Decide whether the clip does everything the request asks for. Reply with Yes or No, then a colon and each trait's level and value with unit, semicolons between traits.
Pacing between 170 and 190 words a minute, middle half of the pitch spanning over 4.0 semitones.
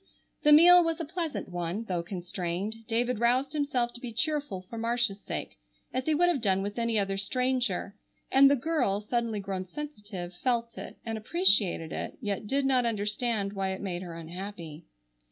Yes: average, 180 wpm; average, 5.1 semitones